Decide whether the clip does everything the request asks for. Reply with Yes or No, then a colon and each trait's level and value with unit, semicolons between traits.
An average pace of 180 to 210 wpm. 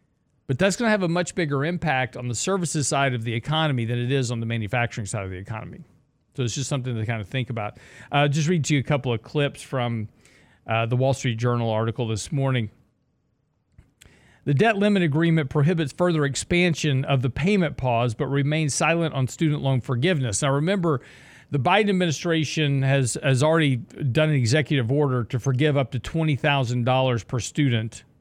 Yes: average, 195 wpm